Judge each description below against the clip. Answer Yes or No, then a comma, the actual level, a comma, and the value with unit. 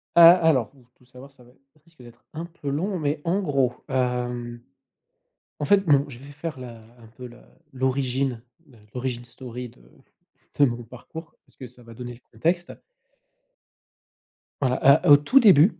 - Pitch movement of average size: Yes, average, 3.8 semitones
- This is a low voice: Yes, low, 130 Hz